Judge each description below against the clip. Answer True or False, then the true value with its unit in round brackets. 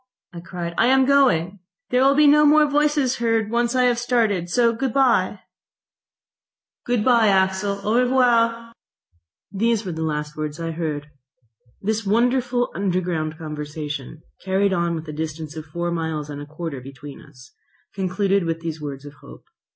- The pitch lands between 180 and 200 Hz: True (190 Hz)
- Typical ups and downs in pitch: False (7.1 semitones)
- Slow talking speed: False (165 wpm)